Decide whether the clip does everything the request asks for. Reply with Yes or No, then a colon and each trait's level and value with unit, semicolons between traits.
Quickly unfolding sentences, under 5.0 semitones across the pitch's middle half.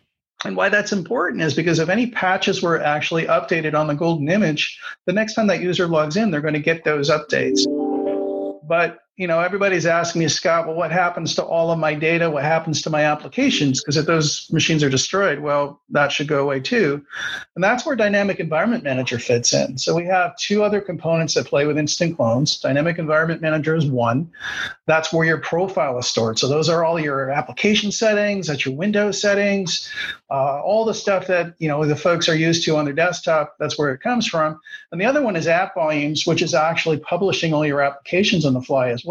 Yes: fast, 215 wpm; average, 3.6 semitones